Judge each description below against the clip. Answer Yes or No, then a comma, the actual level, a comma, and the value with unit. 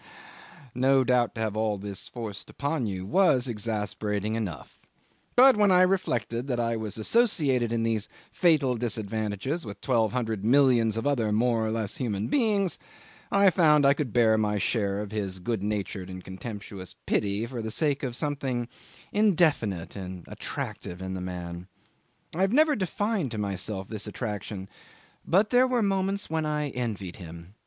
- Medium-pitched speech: No, low, 115 Hz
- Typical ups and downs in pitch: No, wide, 6.2 semitones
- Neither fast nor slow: Yes, average, 165 wpm